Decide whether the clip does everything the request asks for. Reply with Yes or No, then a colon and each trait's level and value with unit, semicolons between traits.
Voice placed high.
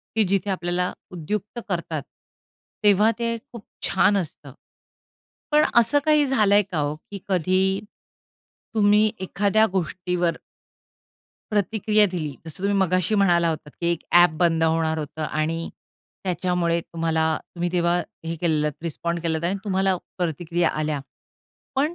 No: medium, 180 Hz